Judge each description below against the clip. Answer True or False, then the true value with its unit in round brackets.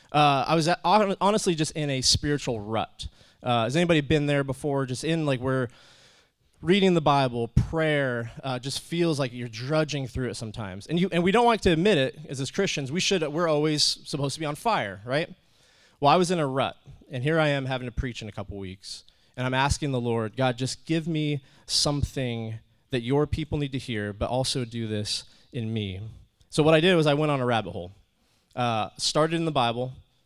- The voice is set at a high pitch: False (135 Hz)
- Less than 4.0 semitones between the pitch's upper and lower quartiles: False (4.6 semitones)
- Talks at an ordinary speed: False (220 wpm)